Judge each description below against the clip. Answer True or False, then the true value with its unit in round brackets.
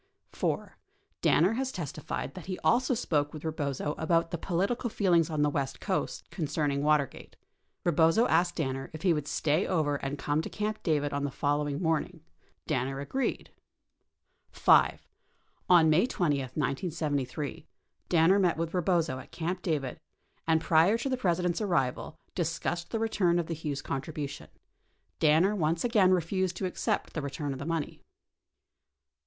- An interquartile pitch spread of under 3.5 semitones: False (3.8 semitones)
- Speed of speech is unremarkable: True (155 wpm)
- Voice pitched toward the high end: False (160 Hz)